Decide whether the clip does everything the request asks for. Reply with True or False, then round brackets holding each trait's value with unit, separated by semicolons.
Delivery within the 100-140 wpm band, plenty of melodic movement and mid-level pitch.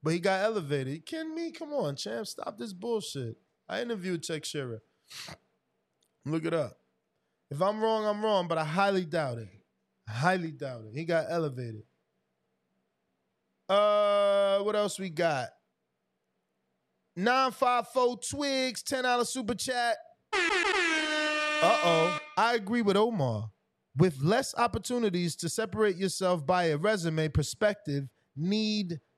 False (135 wpm; 7.0 semitones; 195 Hz)